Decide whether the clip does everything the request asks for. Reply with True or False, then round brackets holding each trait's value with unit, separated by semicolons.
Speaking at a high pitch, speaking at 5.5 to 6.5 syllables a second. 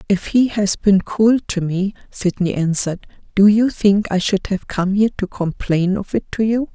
False (200 Hz; 4.7 syllables/s)